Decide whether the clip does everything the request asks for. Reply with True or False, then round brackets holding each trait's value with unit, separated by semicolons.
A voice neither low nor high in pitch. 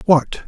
True (160 Hz)